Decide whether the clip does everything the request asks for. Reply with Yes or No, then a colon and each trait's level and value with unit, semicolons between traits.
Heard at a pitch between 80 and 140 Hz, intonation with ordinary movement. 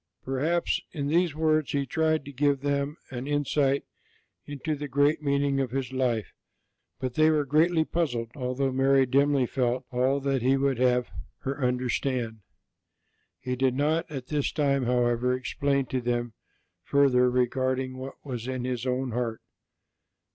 No: low, 135 Hz; narrow, 2.2 semitones